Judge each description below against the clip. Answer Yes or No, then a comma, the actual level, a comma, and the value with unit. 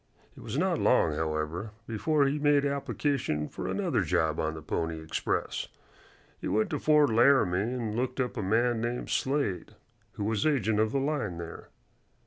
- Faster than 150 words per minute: Yes, average, 170 wpm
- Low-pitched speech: Yes, low, 110 Hz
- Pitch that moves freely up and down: Yes, wide, 7.8 semitones